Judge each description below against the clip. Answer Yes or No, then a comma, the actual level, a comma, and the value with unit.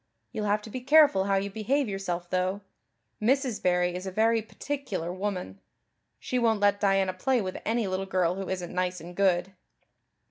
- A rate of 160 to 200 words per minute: Yes, average, 180 wpm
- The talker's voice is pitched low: No, high, 195 Hz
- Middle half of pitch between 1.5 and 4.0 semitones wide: Yes, average, 3.3 semitones